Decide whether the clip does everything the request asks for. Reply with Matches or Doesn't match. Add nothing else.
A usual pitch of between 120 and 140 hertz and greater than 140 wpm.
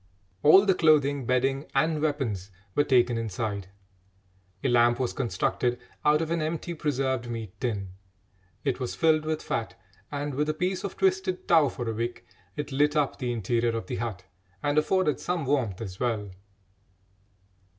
Matches